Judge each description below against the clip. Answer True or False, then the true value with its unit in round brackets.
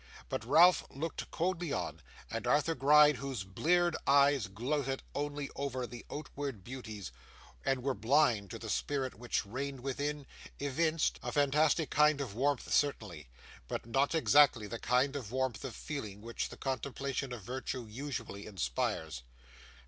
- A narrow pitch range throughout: False (3.8 semitones)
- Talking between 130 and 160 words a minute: True (150 wpm)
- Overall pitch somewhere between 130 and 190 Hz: True (135 Hz)